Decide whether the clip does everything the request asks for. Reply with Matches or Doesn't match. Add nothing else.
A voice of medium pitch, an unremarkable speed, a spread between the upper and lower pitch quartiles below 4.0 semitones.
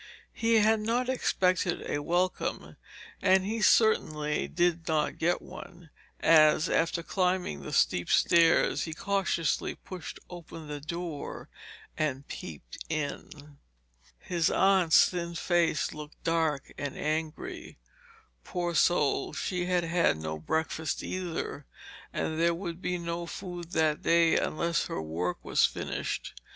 Doesn't match